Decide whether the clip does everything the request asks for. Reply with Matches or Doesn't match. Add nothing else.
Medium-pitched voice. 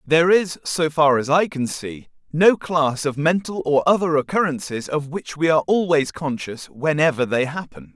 Matches